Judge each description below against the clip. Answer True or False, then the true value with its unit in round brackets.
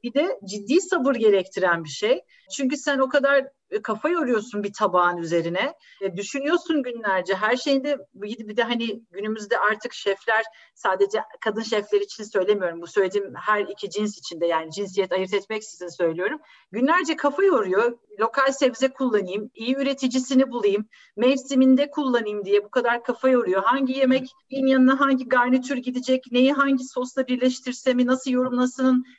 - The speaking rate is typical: False (145 wpm)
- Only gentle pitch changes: False (4.5 semitones)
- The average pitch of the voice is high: True (245 Hz)